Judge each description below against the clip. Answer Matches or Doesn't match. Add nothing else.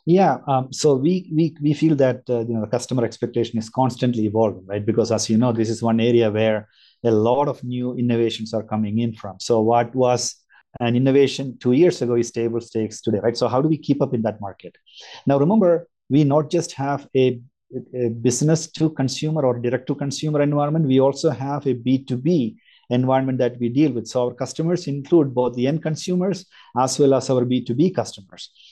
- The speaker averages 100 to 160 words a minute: Doesn't match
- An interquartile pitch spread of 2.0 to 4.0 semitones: Matches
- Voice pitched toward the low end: Matches